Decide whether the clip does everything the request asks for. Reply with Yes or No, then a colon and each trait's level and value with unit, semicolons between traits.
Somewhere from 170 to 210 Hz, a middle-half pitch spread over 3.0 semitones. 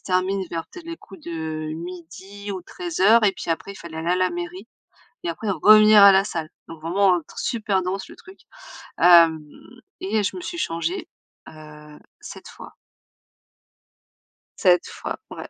Yes: medium, 185 Hz; average, 3.5 semitones